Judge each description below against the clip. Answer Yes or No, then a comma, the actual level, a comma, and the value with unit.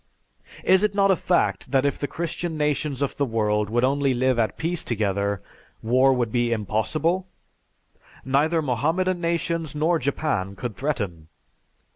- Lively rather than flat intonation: Yes, wide, 6.1 semitones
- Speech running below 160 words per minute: Yes, average, 150 wpm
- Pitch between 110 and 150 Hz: Yes, medium, 140 Hz